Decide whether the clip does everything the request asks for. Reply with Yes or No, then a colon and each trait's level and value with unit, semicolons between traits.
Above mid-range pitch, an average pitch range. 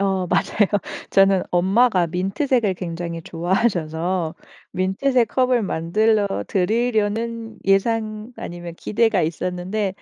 Yes: high, 195 Hz; average, 4.0 semitones